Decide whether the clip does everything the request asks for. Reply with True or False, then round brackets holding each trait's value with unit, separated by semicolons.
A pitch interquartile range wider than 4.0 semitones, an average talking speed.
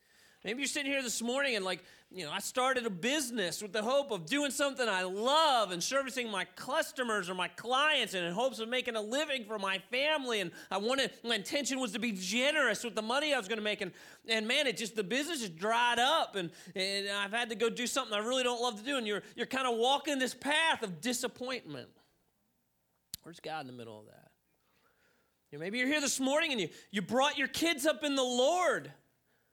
False (5.2 semitones; 230 wpm)